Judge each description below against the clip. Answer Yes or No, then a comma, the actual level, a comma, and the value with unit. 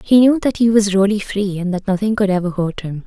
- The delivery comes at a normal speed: No, fast, 275 wpm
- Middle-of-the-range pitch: No, high, 200 Hz